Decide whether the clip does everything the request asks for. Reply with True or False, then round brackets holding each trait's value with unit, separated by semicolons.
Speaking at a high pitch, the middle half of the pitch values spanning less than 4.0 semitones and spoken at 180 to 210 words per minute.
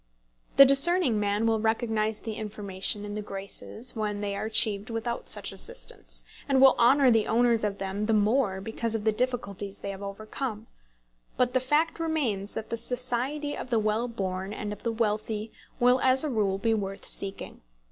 True (220 Hz; 3.2 semitones; 185 wpm)